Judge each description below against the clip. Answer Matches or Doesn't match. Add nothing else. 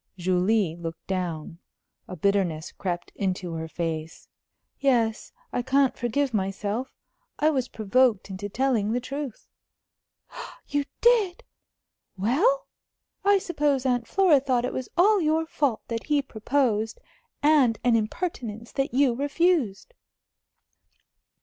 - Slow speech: Matches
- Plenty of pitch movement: Matches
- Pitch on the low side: Doesn't match